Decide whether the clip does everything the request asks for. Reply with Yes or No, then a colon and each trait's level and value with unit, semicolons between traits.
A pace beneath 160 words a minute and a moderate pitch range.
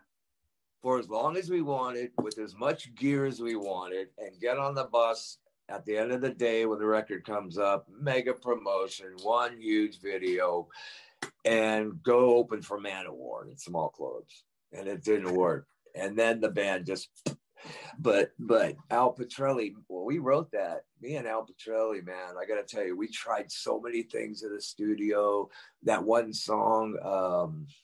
No: average, 175 wpm; average, 4.6 semitones